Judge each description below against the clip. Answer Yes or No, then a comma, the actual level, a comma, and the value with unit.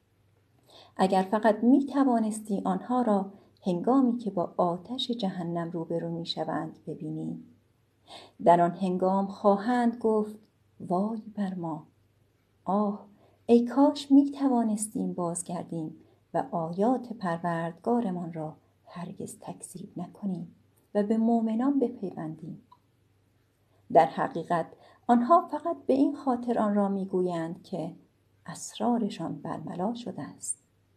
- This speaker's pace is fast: No, slow, 105 wpm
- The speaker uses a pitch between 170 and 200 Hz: Yes, medium, 185 Hz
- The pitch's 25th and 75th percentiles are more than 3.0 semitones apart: Yes, average, 5.3 semitones